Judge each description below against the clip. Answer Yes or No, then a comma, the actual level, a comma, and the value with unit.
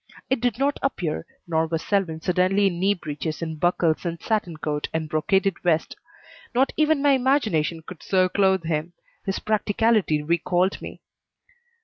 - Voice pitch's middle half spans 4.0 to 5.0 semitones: Yes, average, 4.4 semitones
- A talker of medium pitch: Yes, medium, 180 Hz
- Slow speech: No, average, 155 wpm